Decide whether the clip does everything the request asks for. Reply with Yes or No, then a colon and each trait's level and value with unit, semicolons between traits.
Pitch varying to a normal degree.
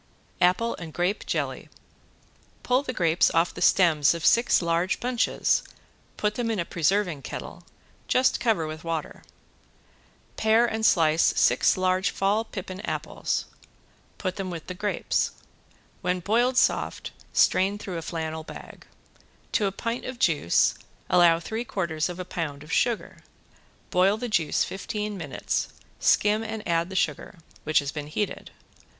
Yes: average, 4.6 semitones